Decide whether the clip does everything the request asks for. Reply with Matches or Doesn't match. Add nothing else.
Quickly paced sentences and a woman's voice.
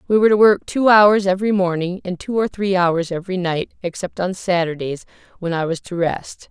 Matches